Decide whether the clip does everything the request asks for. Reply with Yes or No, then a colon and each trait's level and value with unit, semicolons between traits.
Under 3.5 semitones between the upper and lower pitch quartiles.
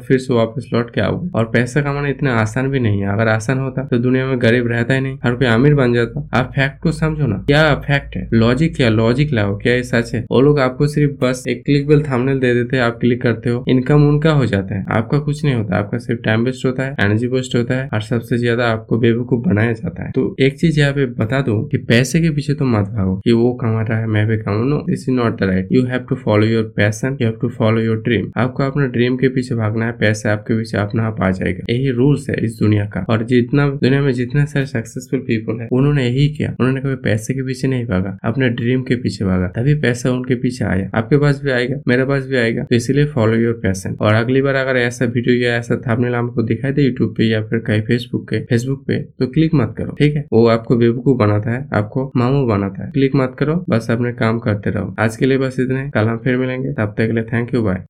Yes: average, 3.1 semitones